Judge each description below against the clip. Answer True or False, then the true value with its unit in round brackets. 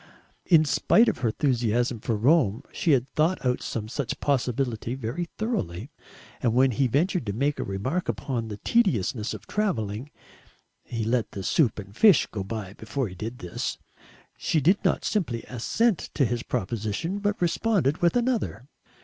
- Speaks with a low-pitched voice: True (125 Hz)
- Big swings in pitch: True (7.0 semitones)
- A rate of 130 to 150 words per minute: False (165 wpm)